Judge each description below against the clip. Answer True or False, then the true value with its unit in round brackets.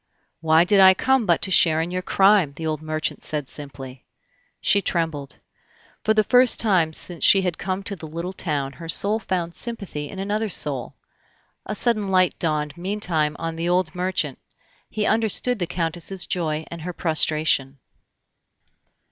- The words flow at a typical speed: True (165 wpm)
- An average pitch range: True (3.8 semitones)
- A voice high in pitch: False (175 Hz)